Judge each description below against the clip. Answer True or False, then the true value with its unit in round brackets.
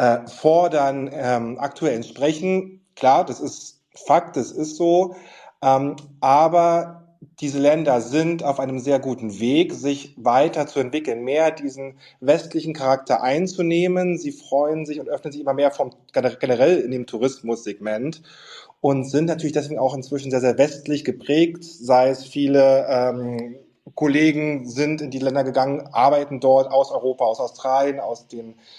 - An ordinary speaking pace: True (150 wpm)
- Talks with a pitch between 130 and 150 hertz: True (140 Hz)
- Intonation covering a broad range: False (2.8 semitones)